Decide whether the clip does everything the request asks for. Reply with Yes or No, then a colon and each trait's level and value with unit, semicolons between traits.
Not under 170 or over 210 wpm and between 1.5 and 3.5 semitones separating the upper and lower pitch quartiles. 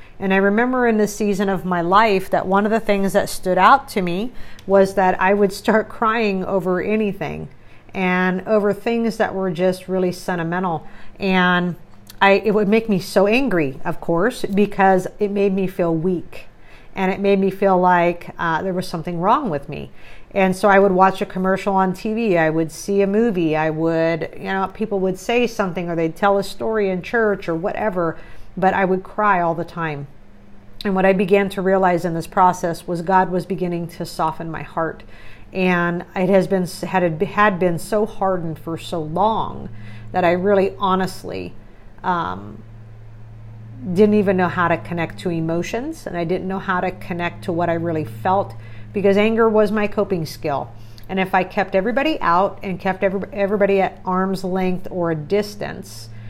Yes: average, 190 wpm; average, 2.9 semitones